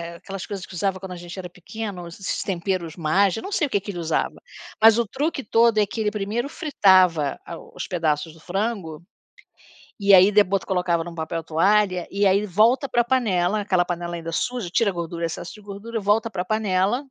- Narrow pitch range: No, average, 3.6 semitones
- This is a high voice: Yes, high, 195 Hz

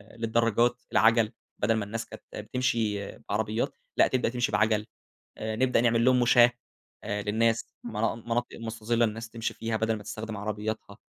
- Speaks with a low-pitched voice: Yes, low, 115 Hz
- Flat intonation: Yes, narrow, 1.5 semitones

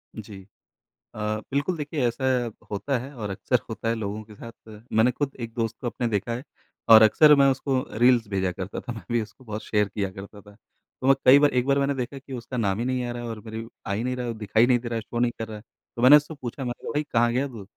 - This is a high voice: No, low, 120 Hz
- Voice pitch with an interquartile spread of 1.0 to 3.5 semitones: Yes, average, 3.1 semitones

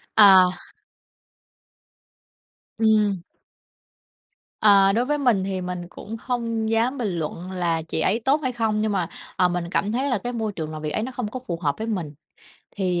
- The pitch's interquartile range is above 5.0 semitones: No, average, 4.3 semitones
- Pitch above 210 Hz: No, high, 205 Hz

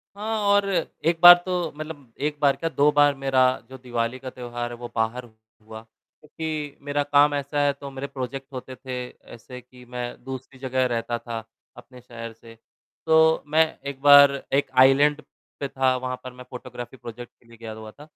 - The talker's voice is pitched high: No, low, 130 Hz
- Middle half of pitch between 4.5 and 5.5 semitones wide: No, average, 3.1 semitones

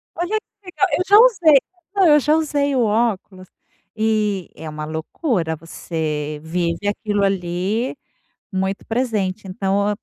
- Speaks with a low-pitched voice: No, high, 205 Hz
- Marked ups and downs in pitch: Yes, wide, 8.1 semitones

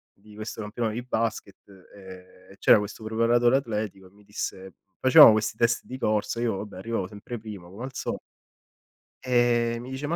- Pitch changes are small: No, average, 3.1 semitones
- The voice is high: No, low, 110 Hz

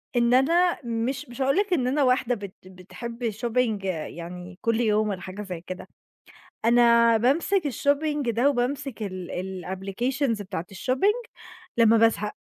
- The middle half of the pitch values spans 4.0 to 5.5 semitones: Yes, average, 5.0 semitones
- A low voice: No, high, 235 Hz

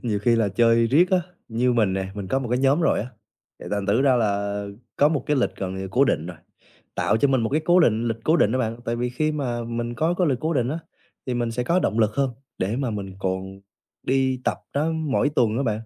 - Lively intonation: No, average, 4.6 semitones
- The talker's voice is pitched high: No, low, 120 Hz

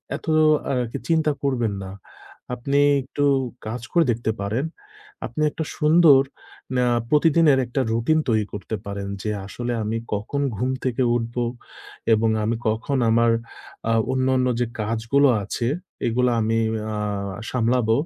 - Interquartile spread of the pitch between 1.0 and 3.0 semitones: No, average, 3.4 semitones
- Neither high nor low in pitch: No, low, 120 Hz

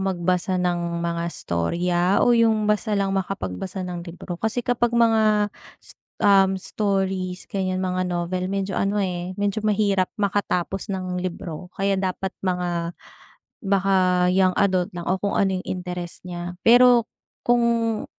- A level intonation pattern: Yes, narrow, 2.2 semitones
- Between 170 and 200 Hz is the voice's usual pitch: Yes, high, 190 Hz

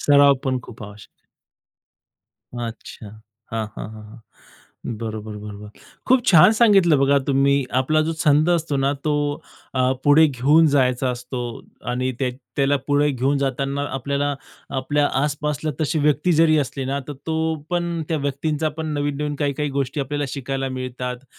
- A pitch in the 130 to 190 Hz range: Yes, medium, 140 Hz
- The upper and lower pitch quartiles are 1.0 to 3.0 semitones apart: Yes, narrow, 2.6 semitones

